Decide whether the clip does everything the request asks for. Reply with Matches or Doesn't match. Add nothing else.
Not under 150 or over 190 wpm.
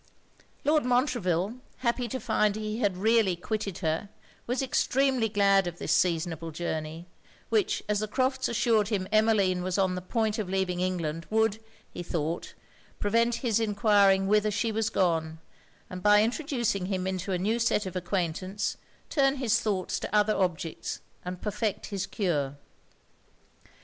Matches